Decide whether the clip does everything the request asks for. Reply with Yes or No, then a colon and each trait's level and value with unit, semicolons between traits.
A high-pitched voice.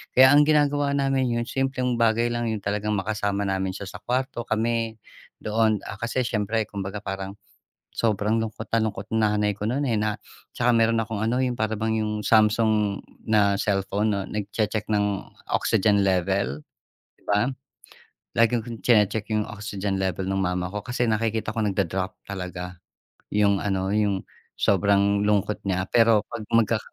No: low, 105 Hz